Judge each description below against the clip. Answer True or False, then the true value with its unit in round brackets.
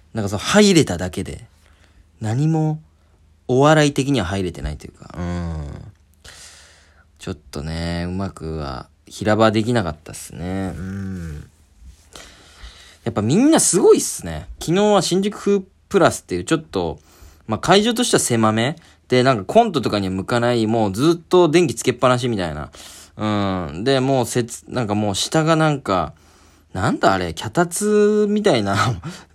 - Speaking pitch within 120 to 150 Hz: False (105 Hz)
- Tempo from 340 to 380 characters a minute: False (315 characters per minute)